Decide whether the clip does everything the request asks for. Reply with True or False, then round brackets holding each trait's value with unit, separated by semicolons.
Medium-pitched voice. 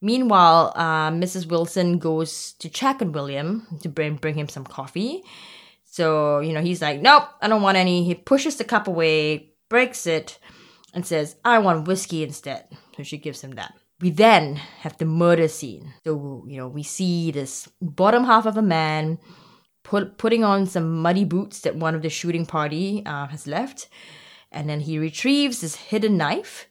True (165 Hz)